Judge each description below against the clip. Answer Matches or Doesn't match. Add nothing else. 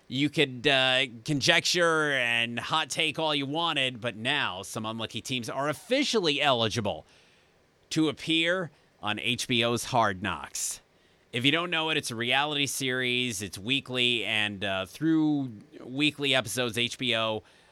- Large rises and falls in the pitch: Doesn't match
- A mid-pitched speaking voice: Doesn't match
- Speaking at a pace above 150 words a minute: Doesn't match